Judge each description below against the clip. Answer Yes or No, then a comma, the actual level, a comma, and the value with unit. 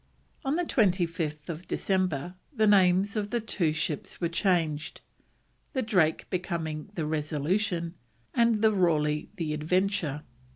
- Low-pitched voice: No, medium, 175 Hz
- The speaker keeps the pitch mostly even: No, average, 4.7 semitones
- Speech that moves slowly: Yes, slow, 120 wpm